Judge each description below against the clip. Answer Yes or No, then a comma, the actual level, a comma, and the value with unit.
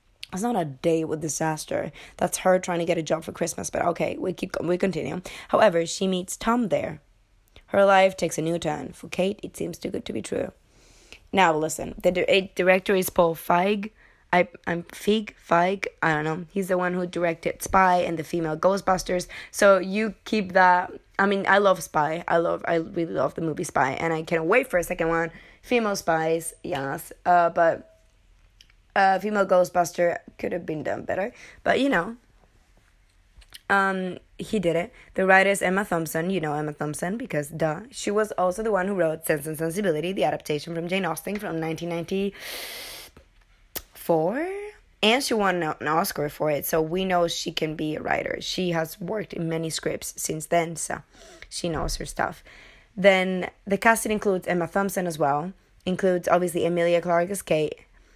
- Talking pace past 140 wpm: Yes, average, 185 wpm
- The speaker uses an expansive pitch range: No, average, 3.0 semitones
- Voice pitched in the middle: Yes, medium, 175 Hz